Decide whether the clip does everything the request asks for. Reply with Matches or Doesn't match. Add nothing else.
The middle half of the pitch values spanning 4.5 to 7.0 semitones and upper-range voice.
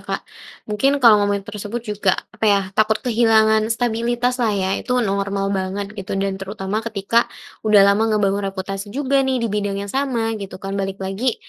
Doesn't match